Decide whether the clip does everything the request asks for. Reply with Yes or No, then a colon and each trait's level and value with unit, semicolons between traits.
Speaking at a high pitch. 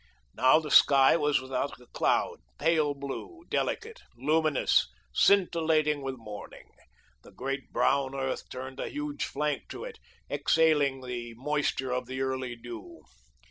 No: medium, 140 Hz